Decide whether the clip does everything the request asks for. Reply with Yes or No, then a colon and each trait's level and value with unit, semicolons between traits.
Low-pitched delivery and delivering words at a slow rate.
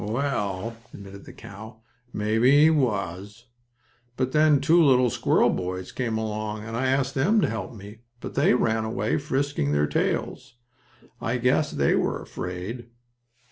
No: low, 115 Hz; average, 150 wpm